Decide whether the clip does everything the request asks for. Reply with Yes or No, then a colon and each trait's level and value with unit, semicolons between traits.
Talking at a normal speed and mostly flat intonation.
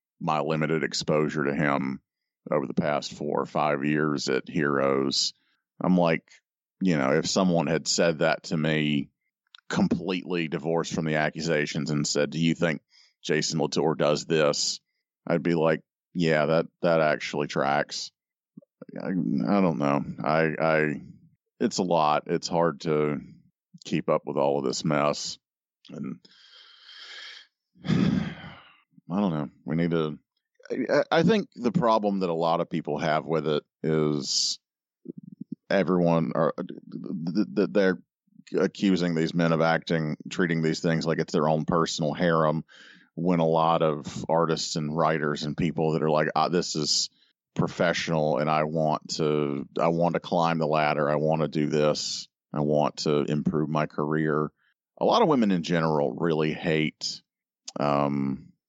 Yes: average, 155 wpm; narrow, 1.8 semitones